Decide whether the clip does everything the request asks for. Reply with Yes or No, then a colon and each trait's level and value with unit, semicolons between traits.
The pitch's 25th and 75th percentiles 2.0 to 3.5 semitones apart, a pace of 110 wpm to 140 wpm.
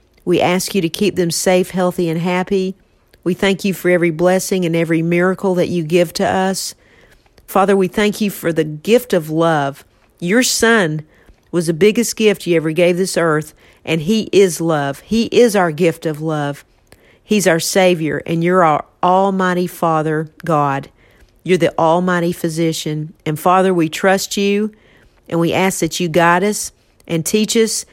No: average, 2.8 semitones; average, 175 wpm